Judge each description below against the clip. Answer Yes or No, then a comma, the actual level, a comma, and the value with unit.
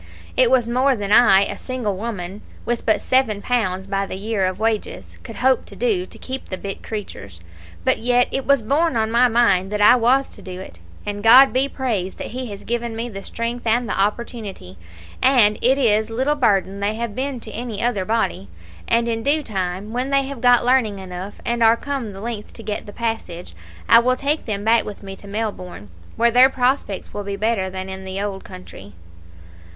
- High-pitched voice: Yes, high, 225 Hz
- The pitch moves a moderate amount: Yes, average, 3.8 semitones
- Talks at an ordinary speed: No, fast, 210 wpm